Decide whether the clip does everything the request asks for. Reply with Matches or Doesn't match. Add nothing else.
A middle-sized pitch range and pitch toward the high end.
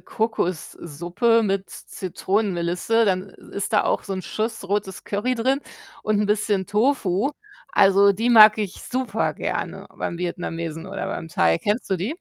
Matches